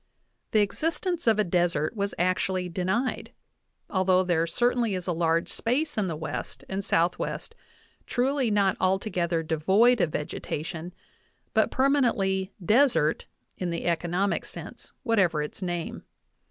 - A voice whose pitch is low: No, high, 190 Hz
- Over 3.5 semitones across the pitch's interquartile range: Yes, average, 5.0 semitones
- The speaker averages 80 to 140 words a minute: Yes, slow, 135 wpm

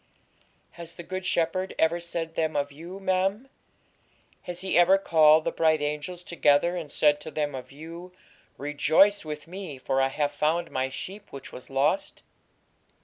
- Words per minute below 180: Yes, average, 165 wpm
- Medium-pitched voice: Yes, medium, 160 Hz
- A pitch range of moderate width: Yes, average, 3.6 semitones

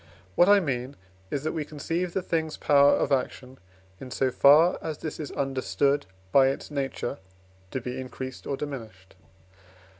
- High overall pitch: No, medium, 140 Hz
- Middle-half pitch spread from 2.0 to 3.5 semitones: Yes, average, 2.9 semitones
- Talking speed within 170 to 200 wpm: No, average, 160 wpm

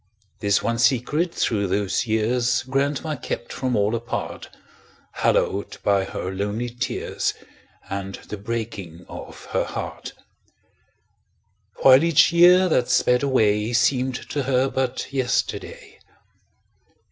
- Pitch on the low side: Yes, low, 120 Hz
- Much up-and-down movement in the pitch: No, average, 4.1 semitones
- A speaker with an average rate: No, slow, 115 wpm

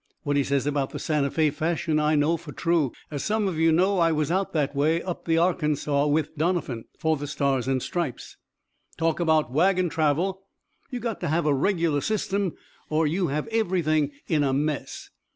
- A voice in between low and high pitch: Yes, medium, 155 Hz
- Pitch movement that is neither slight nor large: Yes, average, 3.0 semitones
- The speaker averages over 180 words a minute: Yes, average, 195 wpm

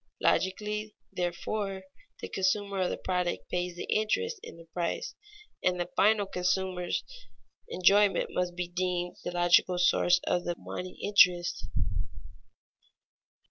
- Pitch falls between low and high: Yes, medium, 180 Hz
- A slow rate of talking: Yes, slow, 125 wpm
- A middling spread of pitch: No, narrow, 2.1 semitones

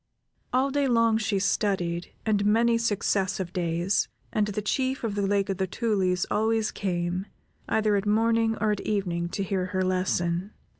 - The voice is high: Yes, high, 205 Hz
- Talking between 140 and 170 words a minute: Yes, average, 165 wpm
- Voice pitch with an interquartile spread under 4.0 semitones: Yes, average, 3.1 semitones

